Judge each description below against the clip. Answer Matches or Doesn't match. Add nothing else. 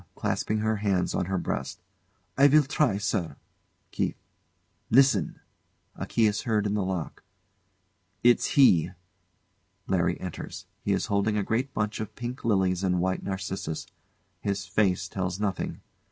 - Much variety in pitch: Doesn't match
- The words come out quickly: Doesn't match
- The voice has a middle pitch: Doesn't match